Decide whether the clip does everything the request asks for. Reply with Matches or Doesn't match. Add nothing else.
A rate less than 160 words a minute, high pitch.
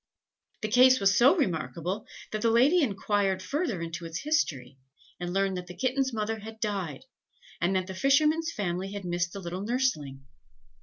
Doesn't match